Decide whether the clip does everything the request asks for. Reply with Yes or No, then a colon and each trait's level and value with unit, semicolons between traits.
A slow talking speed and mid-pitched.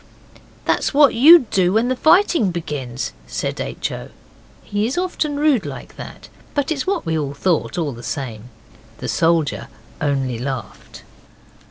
No: average, 160 wpm; medium, 175 Hz